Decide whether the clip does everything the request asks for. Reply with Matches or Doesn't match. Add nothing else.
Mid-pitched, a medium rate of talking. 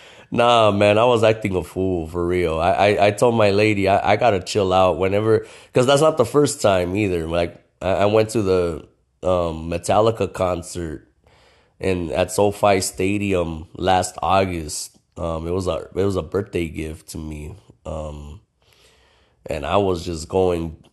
Doesn't match